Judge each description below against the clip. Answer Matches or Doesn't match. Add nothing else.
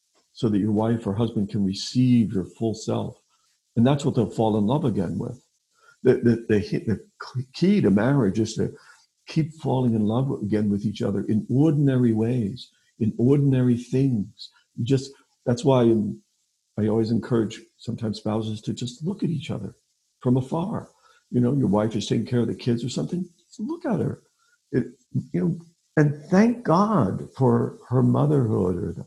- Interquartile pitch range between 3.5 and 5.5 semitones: Matches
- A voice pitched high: Doesn't match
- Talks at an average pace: Matches